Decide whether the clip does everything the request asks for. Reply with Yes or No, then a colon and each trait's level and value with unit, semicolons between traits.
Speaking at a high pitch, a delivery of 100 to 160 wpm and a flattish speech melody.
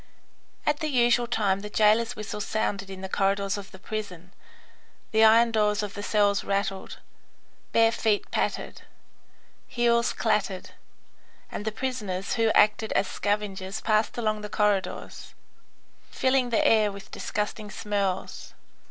Yes: high, 210 Hz; slow, 135 wpm; narrow, 2.2 semitones